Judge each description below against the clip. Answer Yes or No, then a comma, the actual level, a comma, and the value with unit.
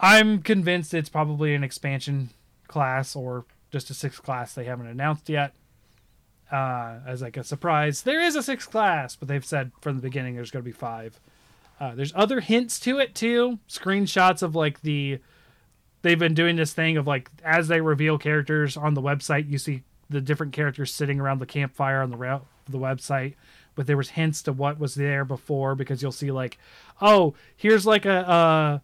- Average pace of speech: Yes, average, 195 wpm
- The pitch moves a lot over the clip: No, average, 3.3 semitones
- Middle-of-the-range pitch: Yes, medium, 145 Hz